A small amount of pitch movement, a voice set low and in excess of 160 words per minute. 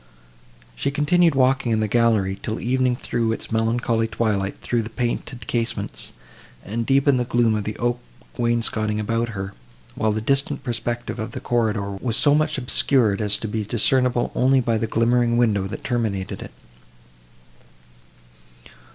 No: narrow, 2.3 semitones; low, 115 Hz; average, 155 wpm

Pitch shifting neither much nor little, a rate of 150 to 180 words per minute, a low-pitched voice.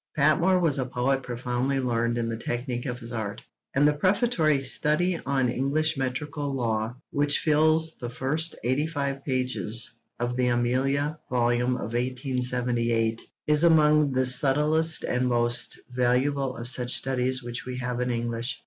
Yes: average, 3.3 semitones; average, 155 wpm; low, 130 Hz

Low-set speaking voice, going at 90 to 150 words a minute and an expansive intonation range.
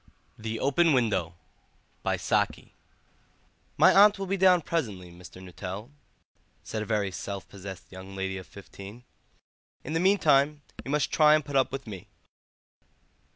Yes: low, 115 Hz; average, 140 wpm; wide, 7.9 semitones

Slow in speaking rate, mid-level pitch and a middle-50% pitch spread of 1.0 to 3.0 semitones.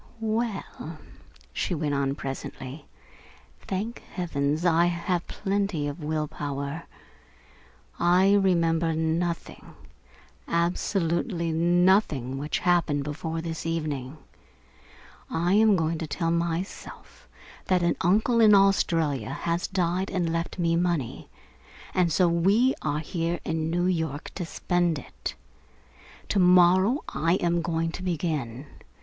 Yes: slow, 120 wpm; medium, 170 Hz; narrow, 2.6 semitones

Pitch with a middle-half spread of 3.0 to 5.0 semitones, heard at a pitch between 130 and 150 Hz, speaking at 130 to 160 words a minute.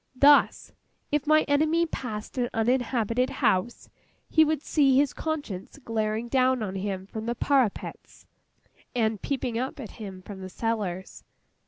No: average, 4.7 semitones; high, 240 Hz; average, 145 wpm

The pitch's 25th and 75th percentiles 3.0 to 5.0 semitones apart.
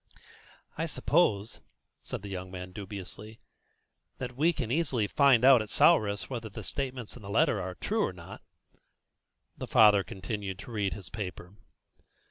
Yes: average, 4.2 semitones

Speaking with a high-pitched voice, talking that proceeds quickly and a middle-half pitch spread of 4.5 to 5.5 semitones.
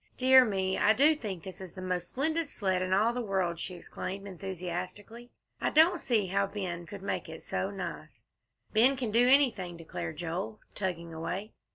No: high, 195 Hz; average, 185 wpm; average, 4.8 semitones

